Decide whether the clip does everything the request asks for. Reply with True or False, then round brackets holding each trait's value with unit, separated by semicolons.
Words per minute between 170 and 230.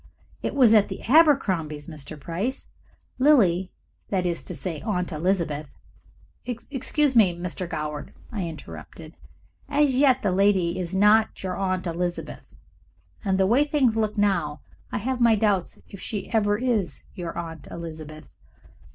False (150 wpm)